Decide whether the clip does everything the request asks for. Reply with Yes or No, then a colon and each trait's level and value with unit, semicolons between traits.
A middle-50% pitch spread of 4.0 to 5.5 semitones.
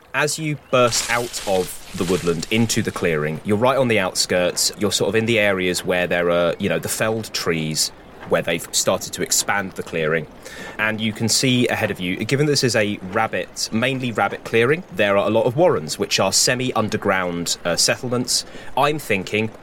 Yes: average, 4.7 semitones